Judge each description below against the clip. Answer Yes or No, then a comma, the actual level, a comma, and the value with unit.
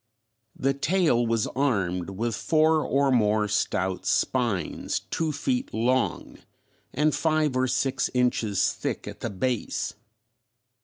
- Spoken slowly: Yes, slow, 120 wpm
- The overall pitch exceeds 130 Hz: No, low, 125 Hz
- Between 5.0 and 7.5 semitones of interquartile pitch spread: Yes, average, 5.3 semitones